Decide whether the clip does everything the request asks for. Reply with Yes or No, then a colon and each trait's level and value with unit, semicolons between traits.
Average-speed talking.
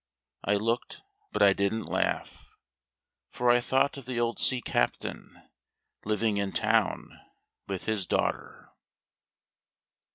No: slow, 120 wpm